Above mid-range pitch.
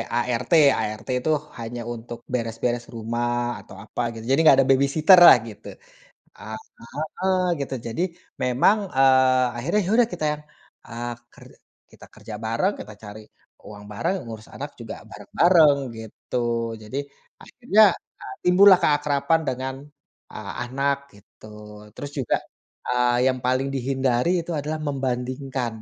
No: low, 130 Hz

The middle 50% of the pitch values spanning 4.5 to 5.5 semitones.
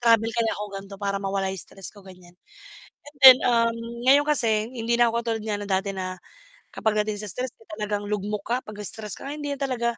No: average, 2.9 semitones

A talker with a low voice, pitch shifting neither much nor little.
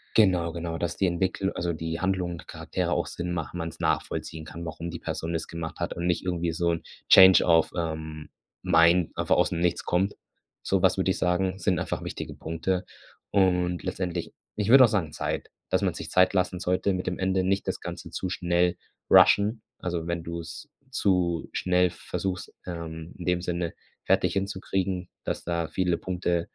No: very low, 90 Hz; narrow, 1.8 semitones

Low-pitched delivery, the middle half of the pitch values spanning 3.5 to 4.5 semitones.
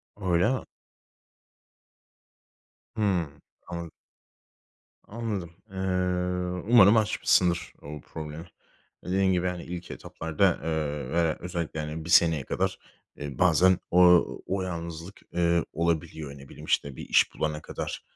No: very low, 85 Hz; average, 2.8 semitones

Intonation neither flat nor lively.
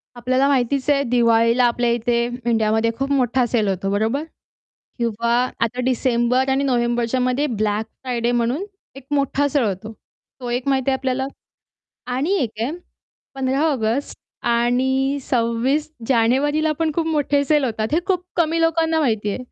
Yes: average, 3.1 semitones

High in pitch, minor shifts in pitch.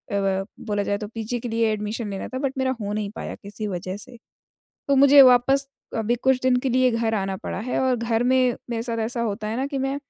No: high, 230 Hz; average, 3.5 semitones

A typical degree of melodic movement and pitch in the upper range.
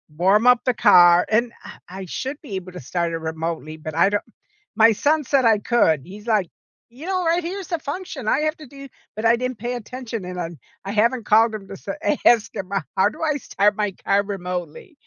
No: wide, 5.9 semitones; high, 215 Hz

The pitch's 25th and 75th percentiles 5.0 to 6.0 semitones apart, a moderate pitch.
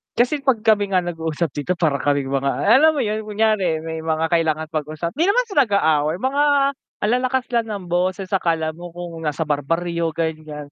Yes: average, 5.3 semitones; medium, 170 Hz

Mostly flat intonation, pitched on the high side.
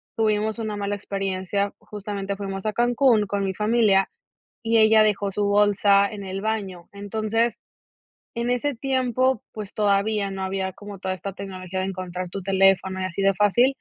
Yes: narrow, 2.1 semitones; high, 200 Hz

